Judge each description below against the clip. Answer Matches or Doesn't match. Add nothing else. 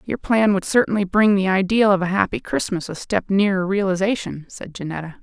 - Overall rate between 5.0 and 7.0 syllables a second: Matches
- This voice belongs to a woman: Matches